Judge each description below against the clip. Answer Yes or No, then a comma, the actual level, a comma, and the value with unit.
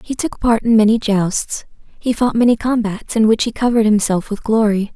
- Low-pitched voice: No, high, 220 Hz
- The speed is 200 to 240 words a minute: Yes, fast, 205 wpm